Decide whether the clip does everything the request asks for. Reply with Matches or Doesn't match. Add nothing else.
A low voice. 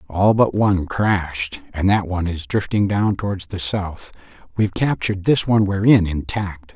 Matches